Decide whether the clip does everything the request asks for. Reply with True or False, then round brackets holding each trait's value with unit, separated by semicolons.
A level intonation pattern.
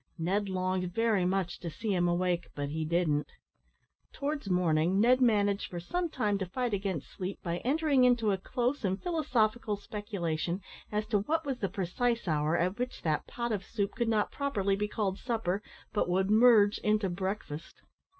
False (4.5 semitones)